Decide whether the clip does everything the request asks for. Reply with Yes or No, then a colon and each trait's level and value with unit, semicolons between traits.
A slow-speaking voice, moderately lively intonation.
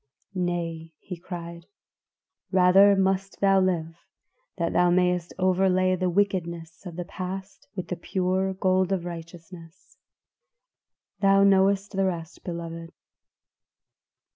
No: slow, 115 wpm; narrow, 2.0 semitones